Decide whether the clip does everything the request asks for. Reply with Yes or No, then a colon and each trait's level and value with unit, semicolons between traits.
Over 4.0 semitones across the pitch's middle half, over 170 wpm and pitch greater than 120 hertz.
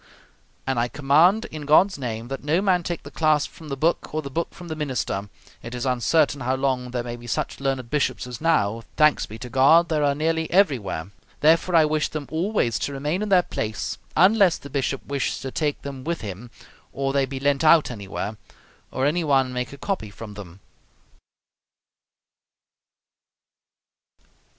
Yes: average, 4.4 semitones; average, 185 wpm; medium, 140 Hz